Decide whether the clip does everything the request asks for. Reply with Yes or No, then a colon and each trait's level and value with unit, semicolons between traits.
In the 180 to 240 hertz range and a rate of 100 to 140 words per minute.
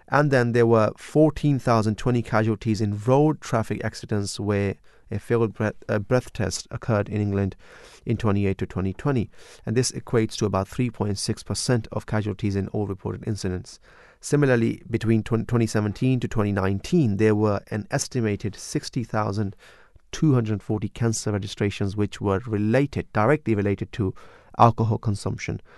No: low, 110 Hz; slow, 135 wpm